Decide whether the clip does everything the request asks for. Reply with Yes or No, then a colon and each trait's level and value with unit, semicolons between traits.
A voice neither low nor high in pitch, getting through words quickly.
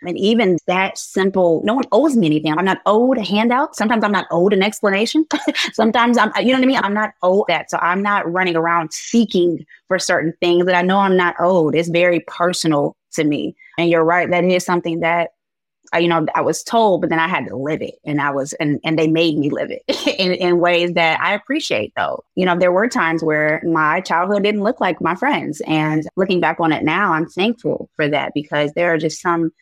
Yes: medium, 175 Hz; fast, 235 wpm